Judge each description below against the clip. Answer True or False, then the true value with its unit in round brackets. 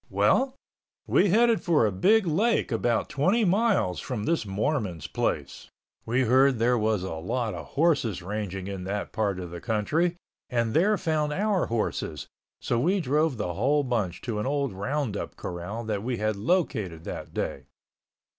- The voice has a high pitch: False (120 Hz)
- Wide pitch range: True (7.8 semitones)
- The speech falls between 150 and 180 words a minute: True (165 wpm)